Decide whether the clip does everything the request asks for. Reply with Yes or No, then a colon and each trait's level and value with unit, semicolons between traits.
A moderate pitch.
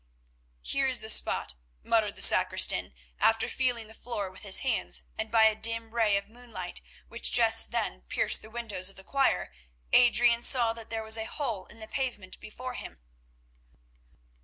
No: high, 225 Hz